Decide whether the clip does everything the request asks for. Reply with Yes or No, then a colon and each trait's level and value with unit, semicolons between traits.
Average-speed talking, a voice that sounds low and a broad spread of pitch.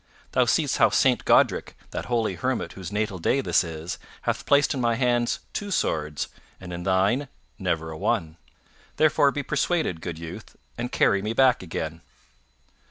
Yes: average, 165 wpm; low, 100 Hz; wide, 7.4 semitones